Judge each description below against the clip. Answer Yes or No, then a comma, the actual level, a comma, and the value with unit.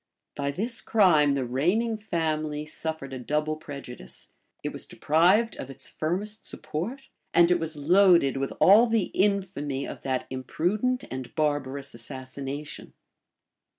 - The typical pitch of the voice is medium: Yes, medium, 155 Hz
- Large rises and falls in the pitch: Yes, wide, 5.8 semitones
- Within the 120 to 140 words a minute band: Yes, slow, 135 wpm